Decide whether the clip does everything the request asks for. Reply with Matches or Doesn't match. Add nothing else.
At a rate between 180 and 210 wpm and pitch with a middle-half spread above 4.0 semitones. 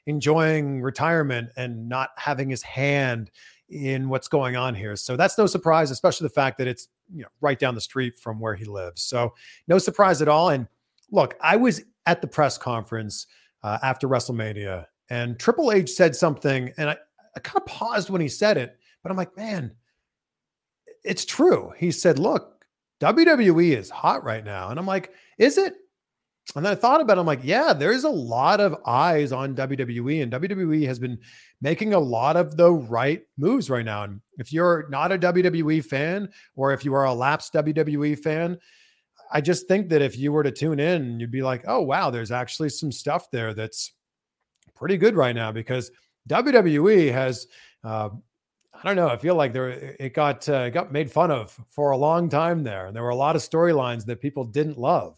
Matches